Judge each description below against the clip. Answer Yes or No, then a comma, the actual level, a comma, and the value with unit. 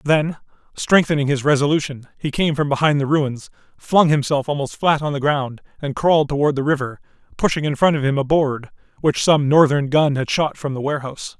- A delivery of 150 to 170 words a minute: No, average, 200 wpm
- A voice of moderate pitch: Yes, medium, 145 Hz